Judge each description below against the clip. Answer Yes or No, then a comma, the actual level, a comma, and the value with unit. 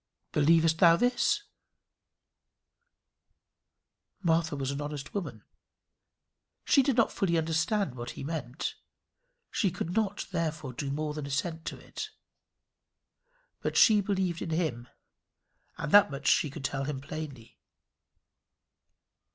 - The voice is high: No, medium, 160 Hz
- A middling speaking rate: No, slow, 120 wpm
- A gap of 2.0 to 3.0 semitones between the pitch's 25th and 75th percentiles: No, average, 4.2 semitones